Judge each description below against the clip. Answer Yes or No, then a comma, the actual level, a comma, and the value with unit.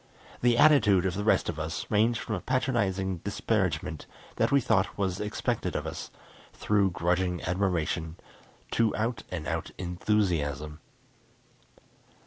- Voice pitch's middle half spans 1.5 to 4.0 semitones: Yes, average, 3.7 semitones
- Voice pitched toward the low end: Yes, very low, 95 Hz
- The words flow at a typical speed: No, slow, 130 wpm